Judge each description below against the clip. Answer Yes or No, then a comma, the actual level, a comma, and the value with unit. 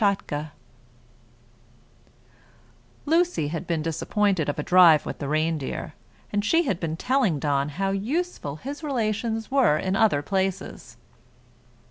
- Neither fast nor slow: No, slow, 125 wpm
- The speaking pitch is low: No, high, 190 Hz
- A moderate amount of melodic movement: No, wide, 6.5 semitones